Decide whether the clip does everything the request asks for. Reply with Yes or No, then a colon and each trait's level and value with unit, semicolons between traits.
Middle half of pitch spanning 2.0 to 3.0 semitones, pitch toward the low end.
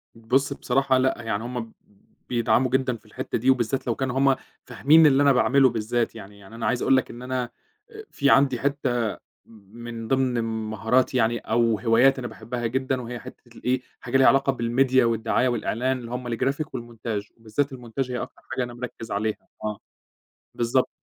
Yes: narrow, 2.5 semitones; low, 125 Hz